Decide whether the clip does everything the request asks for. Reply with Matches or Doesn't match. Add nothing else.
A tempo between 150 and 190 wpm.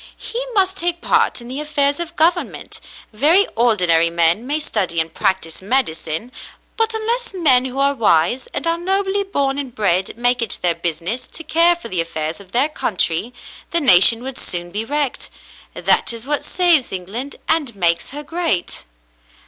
Matches